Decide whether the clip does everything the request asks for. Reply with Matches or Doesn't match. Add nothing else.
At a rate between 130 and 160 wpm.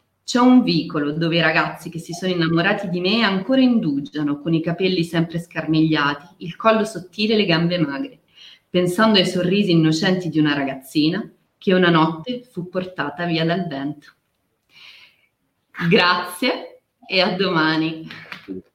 Matches